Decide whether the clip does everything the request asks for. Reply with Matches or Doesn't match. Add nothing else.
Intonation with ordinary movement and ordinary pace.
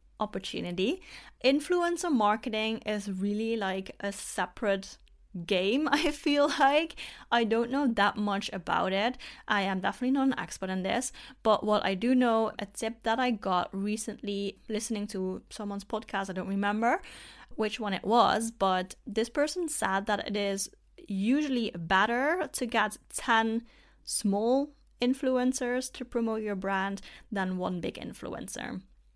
Matches